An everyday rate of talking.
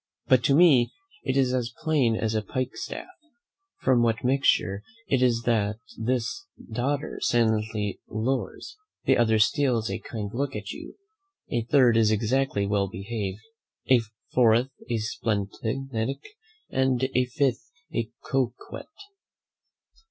No: slow, 130 wpm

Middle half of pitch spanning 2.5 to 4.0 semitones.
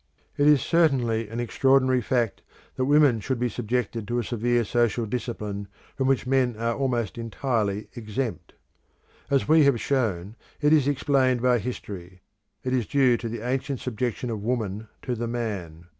Yes: average, 2.9 semitones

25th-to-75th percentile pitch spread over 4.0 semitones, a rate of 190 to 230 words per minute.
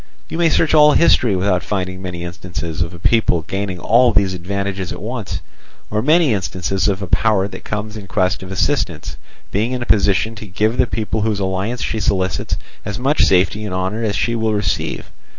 No: average, 3.1 semitones; fast, 205 wpm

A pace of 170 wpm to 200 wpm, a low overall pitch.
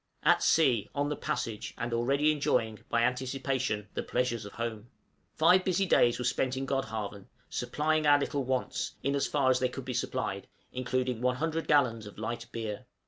Yes: average, 185 wpm; low, 125 Hz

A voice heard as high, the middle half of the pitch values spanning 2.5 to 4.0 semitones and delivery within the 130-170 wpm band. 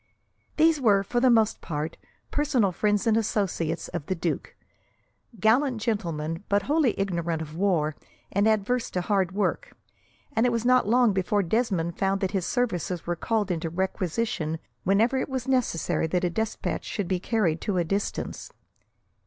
No: high, 200 Hz; average, 4.9 semitones; average, 165 wpm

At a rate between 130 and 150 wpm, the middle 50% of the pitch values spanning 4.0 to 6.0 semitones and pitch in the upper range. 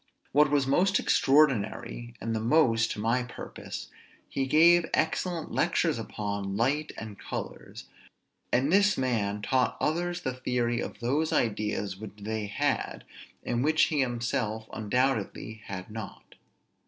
No: average, 140 wpm; average, 5.1 semitones; low, 120 Hz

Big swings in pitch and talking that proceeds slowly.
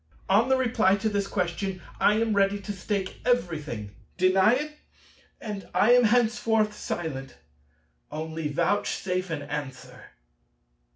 No: average, 4.8 semitones; slow, 125 wpm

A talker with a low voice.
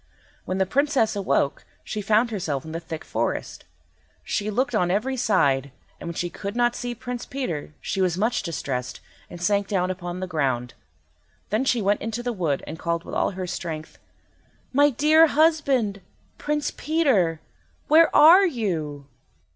No: high, 200 Hz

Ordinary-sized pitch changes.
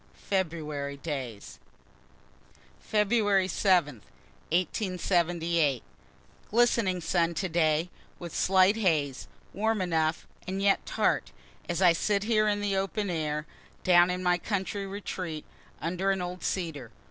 Yes: average, 3.5 semitones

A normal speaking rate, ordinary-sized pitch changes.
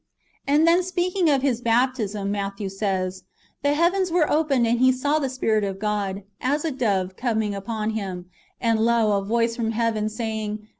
Yes: average, 190 wpm; average, 4.8 semitones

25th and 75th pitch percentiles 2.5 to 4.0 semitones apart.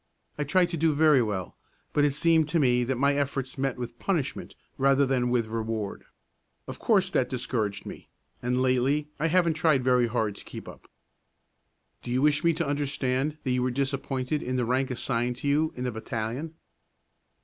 Yes: average, 3.3 semitones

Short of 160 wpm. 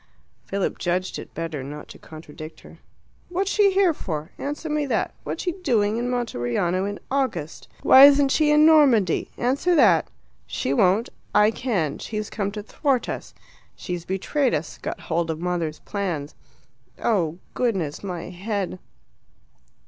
Yes: average, 150 wpm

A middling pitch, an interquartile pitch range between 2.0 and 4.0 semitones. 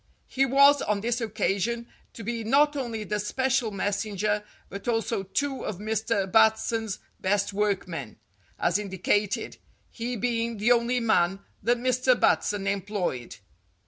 No: high, 220 Hz; average, 3.0 semitones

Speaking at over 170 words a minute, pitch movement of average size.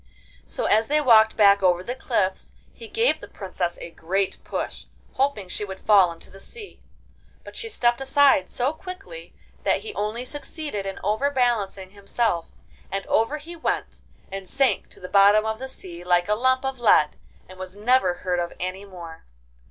No: average, 180 wpm; wide, 6.1 semitones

